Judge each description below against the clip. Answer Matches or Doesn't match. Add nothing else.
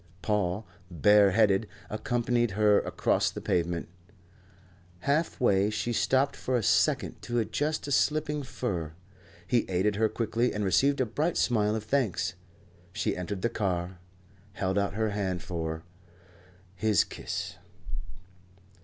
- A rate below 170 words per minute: Matches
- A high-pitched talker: Doesn't match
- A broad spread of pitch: Doesn't match